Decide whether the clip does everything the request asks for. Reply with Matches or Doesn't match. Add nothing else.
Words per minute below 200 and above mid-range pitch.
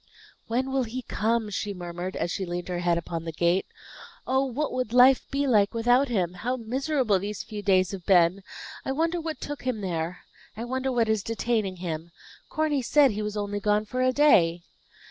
Doesn't match